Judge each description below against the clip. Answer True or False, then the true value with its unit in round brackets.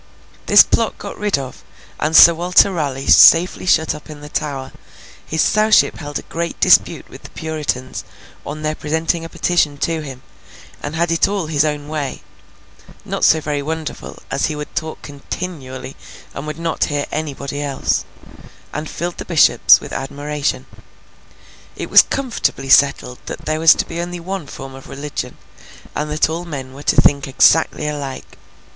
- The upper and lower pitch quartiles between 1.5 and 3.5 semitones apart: True (2.6 semitones)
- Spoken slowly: False (165 wpm)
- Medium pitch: True (150 Hz)